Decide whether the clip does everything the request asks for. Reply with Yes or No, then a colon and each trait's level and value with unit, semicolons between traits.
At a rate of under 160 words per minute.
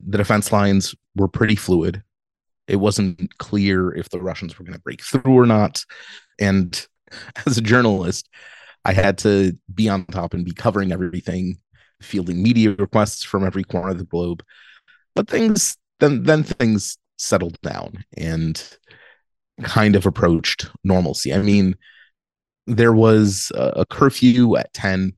Yes: average, 150 wpm